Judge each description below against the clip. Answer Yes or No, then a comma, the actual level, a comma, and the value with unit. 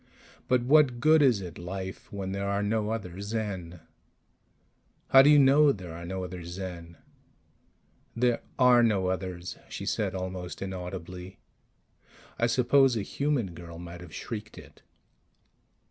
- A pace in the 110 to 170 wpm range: Yes, average, 145 wpm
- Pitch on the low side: Yes, very low, 95 Hz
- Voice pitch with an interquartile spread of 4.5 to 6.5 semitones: Yes, average, 5.1 semitones